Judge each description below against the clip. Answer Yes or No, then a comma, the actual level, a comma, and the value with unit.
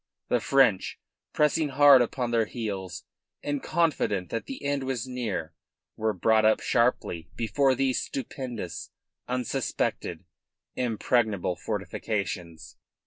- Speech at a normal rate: No, slow, 110 wpm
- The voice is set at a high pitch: No, low, 115 Hz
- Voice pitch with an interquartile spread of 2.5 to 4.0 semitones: No, average, 5.0 semitones